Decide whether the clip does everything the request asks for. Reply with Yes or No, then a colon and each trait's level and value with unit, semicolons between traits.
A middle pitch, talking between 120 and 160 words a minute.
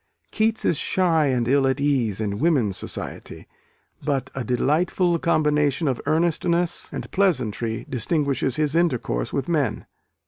Yes: medium, 145 Hz; slow, 135 wpm